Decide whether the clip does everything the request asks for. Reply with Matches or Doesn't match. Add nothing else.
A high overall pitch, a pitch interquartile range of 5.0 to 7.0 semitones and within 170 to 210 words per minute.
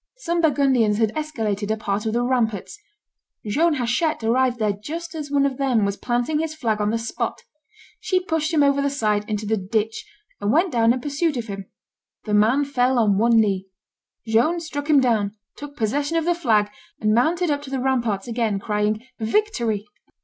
Matches